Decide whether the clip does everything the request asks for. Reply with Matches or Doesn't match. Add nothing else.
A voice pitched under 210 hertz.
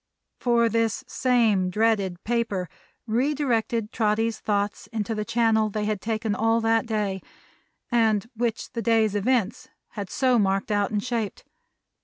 Doesn't match